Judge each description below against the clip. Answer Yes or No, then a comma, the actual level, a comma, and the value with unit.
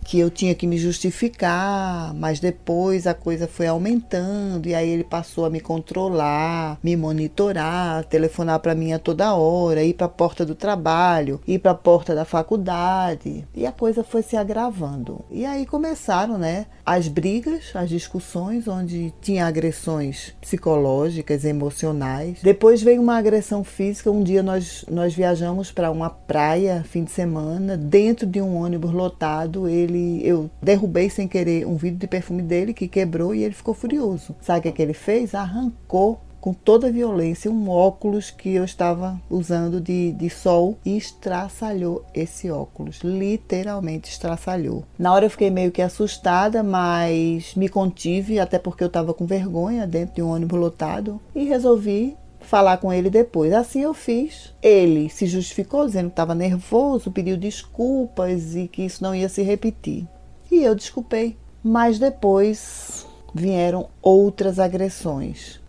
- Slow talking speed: No, average, 160 wpm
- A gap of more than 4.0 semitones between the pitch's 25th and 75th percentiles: No, average, 3.3 semitones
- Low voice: No, medium, 180 Hz